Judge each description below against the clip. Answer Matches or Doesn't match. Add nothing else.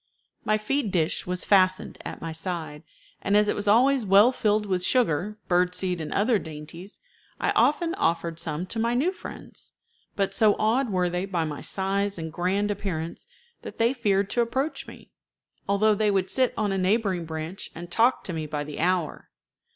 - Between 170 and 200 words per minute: Matches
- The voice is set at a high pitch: Matches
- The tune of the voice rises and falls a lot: Doesn't match